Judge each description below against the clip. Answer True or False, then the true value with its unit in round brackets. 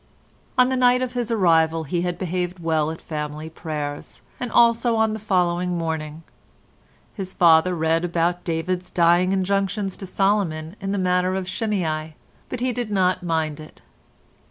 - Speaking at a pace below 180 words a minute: True (160 wpm)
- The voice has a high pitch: False (180 Hz)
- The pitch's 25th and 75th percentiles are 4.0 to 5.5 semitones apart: False (3.5 semitones)